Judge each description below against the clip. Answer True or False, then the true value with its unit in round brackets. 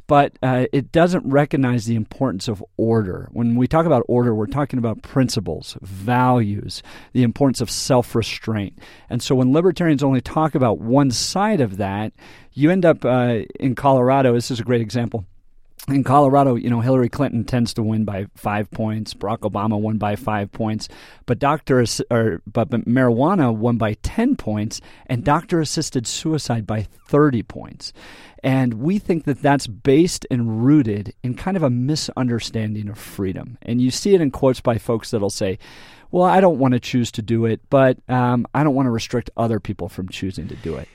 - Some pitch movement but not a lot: True (3.9 semitones)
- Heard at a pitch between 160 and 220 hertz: False (120 Hz)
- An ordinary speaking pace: True (185 wpm)